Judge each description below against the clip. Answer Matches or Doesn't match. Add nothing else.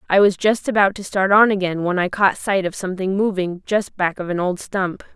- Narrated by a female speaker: Matches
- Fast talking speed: Matches